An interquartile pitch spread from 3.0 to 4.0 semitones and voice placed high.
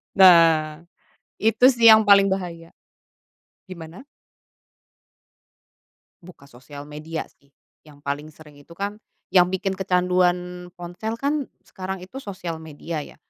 No: average, 3.5 semitones; medium, 180 Hz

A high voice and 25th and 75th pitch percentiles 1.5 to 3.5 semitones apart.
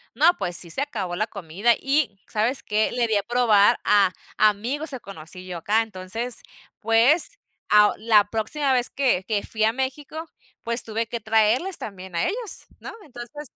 No: high, 225 Hz; average, 4.3 semitones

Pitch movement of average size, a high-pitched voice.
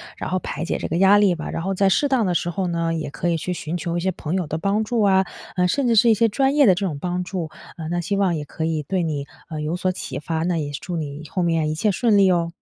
No: average, 3.3 semitones; medium, 175 Hz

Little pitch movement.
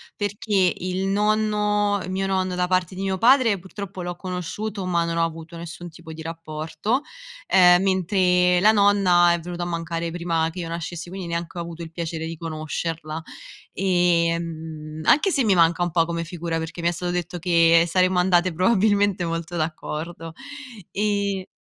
Yes: narrow, 2.3 semitones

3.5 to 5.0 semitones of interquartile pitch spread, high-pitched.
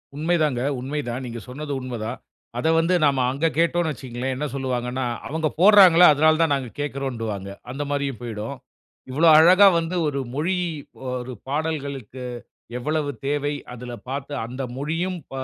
No: average, 3.8 semitones; medium, 140 Hz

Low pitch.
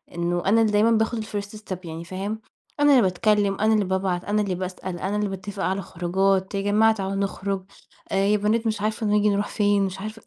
No: high, 200 Hz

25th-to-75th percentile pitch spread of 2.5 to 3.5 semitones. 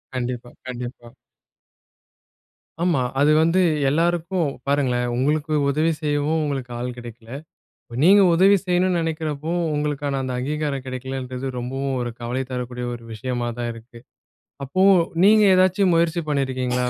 No: average, 4.5 semitones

